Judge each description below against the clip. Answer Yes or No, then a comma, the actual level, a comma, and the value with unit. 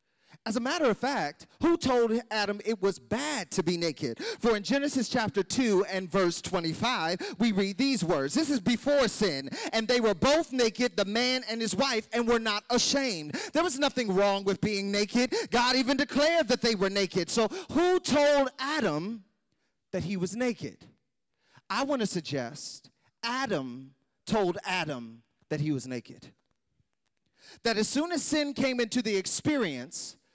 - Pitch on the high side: Yes, high, 225 Hz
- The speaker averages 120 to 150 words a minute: No, average, 170 wpm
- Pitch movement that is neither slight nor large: Yes, average, 5.0 semitones